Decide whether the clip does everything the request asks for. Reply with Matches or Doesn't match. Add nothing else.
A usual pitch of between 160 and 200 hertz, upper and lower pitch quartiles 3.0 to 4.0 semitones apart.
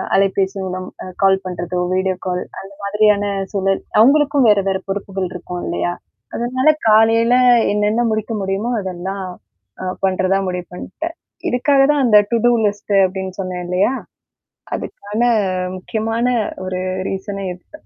Matches